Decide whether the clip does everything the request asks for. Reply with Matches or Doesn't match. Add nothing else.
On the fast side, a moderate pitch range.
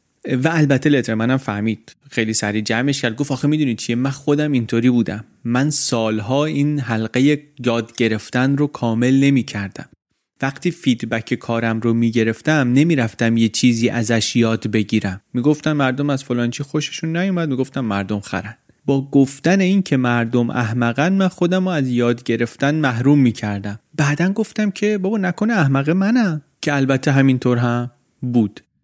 Matches